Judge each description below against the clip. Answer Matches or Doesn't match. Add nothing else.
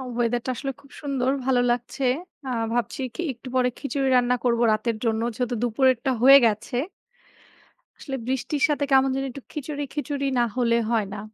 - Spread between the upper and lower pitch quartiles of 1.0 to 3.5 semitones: Matches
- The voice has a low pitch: Doesn't match